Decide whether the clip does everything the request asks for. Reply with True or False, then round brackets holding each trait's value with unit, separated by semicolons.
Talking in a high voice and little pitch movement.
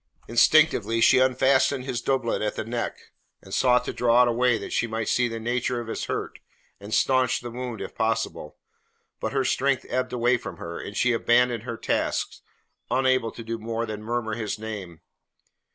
False (120 Hz; 2.1 semitones)